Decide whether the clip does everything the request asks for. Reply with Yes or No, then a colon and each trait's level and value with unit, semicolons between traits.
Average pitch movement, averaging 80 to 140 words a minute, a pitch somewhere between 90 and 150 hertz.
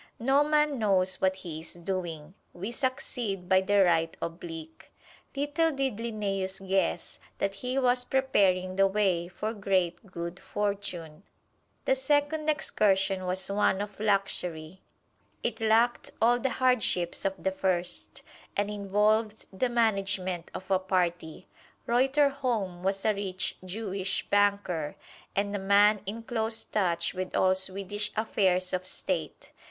No: average, 3.4 semitones; slow, 135 wpm; high, 195 Hz